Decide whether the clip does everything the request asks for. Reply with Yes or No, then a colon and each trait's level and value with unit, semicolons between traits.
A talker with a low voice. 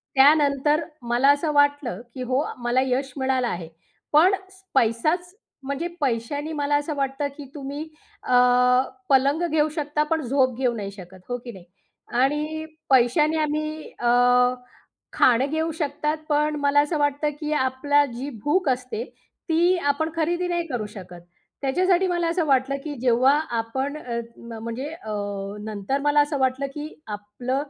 No: very high, 280 Hz